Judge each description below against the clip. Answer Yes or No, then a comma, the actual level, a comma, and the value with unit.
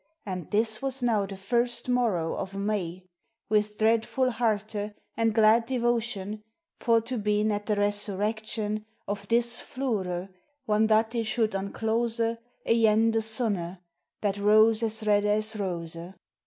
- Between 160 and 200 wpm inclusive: No, average, 140 wpm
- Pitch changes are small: Yes, narrow, 1.9 semitones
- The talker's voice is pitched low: No, high, 215 Hz